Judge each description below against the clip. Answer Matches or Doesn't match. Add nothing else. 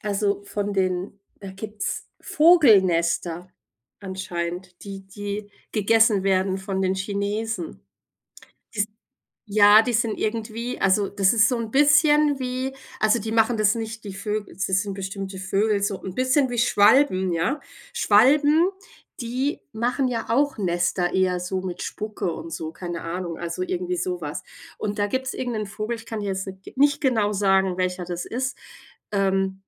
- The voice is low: Doesn't match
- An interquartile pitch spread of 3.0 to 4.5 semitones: Matches